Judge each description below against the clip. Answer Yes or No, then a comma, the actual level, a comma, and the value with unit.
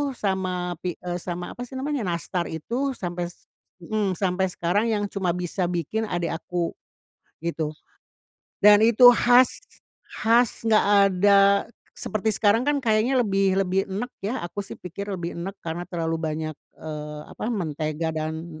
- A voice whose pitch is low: No, medium, 185 Hz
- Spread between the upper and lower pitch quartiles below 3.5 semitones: No, average, 4.1 semitones